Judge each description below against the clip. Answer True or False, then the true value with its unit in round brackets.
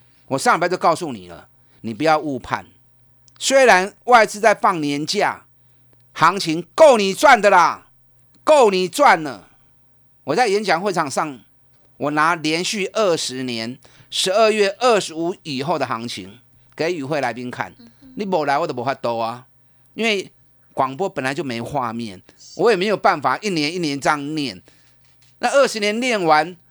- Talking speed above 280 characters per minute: False (230 characters per minute)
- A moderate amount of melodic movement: False (7.7 semitones)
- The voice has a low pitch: False (150 Hz)